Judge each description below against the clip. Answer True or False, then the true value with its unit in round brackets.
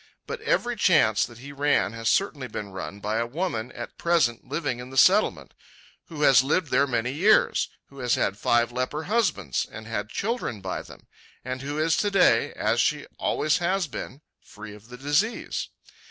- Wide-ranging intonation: True (6.6 semitones)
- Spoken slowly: False (185 wpm)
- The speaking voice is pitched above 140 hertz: False (135 Hz)